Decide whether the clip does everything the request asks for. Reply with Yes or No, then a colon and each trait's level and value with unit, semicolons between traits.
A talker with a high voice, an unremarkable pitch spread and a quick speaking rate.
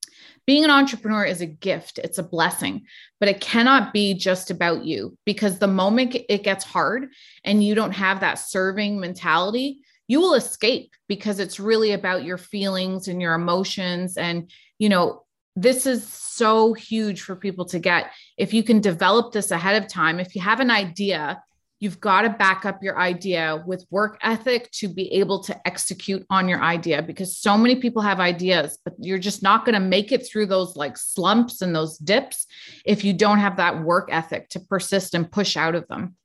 No: high, 195 Hz; average, 3.1 semitones; average, 195 wpm